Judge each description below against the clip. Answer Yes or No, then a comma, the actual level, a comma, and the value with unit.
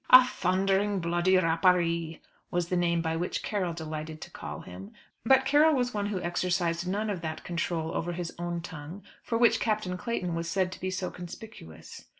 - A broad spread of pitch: No, average, 2.8 semitones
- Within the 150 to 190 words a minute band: Yes, average, 185 wpm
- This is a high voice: No, medium, 175 Hz